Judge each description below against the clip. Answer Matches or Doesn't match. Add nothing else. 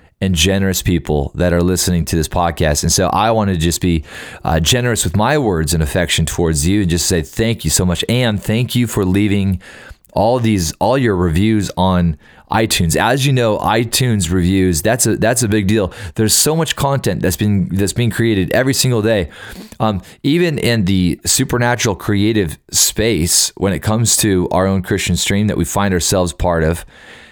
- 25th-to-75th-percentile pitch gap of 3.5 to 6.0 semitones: Matches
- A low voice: Matches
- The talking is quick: Doesn't match